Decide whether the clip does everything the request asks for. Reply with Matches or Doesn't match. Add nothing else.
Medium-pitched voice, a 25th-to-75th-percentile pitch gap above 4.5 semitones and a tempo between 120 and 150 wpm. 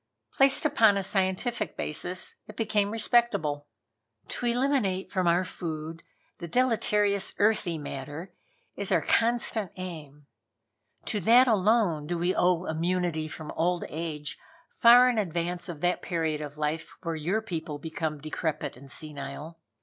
Matches